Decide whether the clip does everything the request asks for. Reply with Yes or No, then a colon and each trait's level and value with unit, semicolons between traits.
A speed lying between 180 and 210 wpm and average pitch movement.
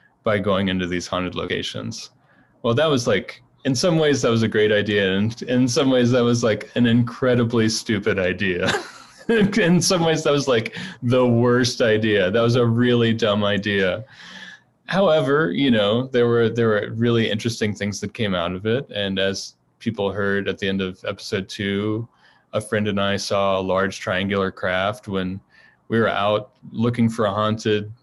Yes: average, 185 wpm; average, 3.4 semitones